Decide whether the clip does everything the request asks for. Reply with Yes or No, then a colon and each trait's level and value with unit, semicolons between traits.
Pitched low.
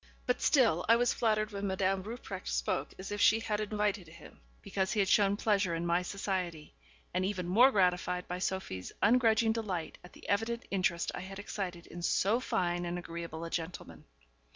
No: high, 190 Hz